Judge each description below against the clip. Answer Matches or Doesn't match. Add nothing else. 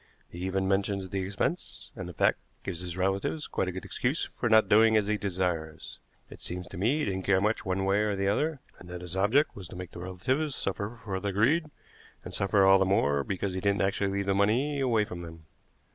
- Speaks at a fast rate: Matches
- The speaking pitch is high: Doesn't match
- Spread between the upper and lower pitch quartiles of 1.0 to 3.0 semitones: Matches